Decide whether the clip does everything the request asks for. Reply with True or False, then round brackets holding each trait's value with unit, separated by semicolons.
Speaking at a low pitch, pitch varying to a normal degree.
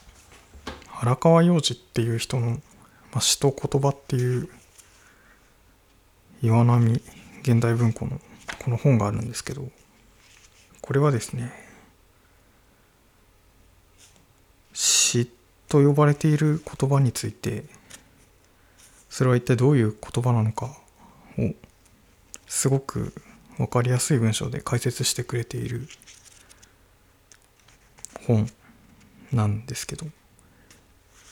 True (115 Hz; 4.7 semitones)